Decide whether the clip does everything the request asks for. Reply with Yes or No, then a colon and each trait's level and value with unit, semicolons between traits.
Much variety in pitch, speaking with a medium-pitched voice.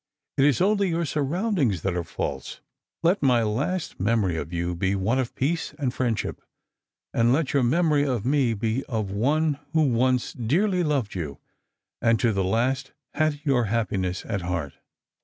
No: wide, 6.6 semitones; low, 125 Hz